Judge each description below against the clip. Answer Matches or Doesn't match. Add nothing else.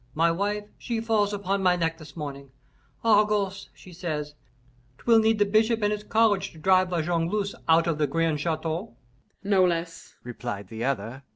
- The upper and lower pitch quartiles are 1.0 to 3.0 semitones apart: Doesn't match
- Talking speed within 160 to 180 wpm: Matches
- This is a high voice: Doesn't match